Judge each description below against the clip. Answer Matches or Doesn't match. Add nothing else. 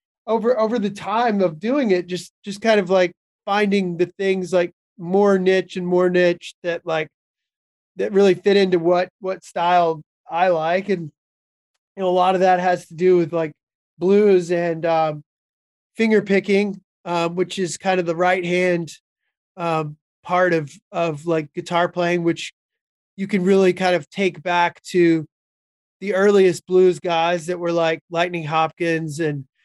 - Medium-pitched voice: Matches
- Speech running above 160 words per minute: Matches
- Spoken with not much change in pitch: Matches